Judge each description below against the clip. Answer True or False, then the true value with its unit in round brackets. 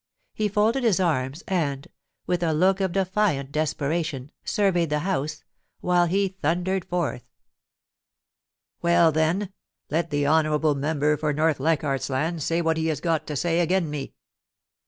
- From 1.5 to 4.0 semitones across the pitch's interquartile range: True (3.1 semitones)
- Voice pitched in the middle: True (160 Hz)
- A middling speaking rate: True (155 wpm)